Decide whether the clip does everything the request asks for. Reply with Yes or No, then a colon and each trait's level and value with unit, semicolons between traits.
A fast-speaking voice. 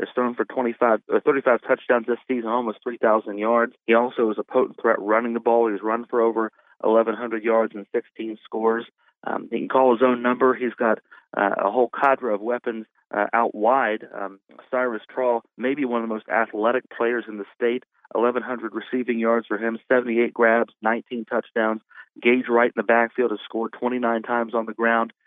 No: average, 195 wpm